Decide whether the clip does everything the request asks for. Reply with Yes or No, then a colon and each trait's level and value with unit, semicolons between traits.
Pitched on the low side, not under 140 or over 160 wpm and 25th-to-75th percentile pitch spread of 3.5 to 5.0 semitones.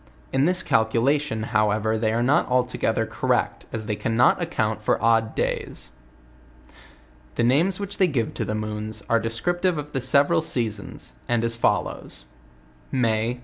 Yes: low, 115 Hz; average, 150 wpm; average, 4.4 semitones